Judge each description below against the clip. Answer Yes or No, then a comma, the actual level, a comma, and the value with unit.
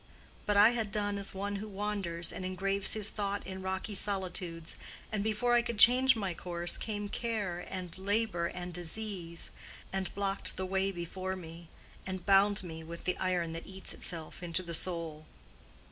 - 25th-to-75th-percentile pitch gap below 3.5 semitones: Yes, average, 2.9 semitones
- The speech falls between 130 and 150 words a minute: No, average, 175 wpm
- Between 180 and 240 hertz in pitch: Yes, high, 190 Hz